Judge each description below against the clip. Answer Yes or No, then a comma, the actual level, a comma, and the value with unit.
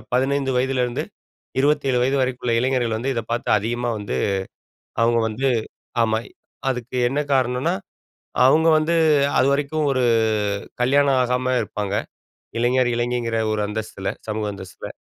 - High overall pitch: No, low, 125 Hz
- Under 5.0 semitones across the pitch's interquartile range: Yes, narrow, 2.6 semitones